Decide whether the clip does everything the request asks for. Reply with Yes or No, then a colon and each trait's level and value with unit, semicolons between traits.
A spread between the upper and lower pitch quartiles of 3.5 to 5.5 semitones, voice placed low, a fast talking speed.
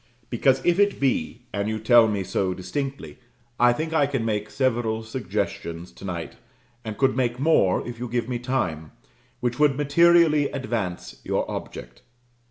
No: average, 4.6 semitones; low, 120 Hz; average, 165 wpm